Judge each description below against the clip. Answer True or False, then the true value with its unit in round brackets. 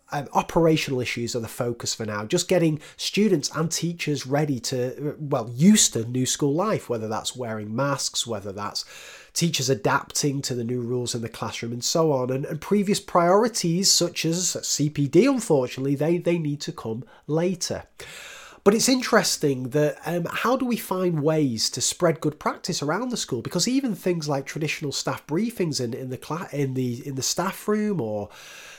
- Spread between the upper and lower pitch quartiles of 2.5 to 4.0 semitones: False (5.6 semitones)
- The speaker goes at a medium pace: True (185 wpm)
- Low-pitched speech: False (150 Hz)